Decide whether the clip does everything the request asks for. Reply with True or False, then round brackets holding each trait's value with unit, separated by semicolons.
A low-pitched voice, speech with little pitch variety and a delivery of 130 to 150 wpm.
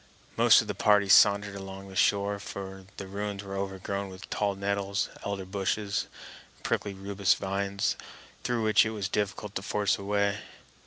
False (100 Hz; 0.8 semitones; 170 wpm)